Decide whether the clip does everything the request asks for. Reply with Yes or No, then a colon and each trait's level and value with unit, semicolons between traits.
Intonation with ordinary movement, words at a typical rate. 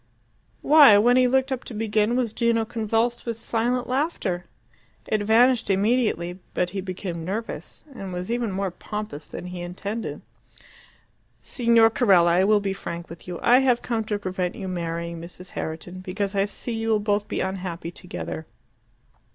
Yes: average, 4.3 semitones; average, 165 wpm